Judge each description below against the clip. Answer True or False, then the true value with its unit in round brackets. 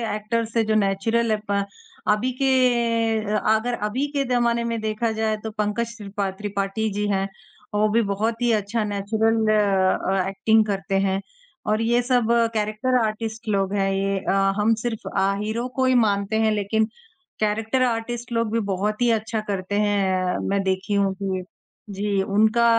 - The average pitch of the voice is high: True (215 Hz)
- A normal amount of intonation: False (2.3 semitones)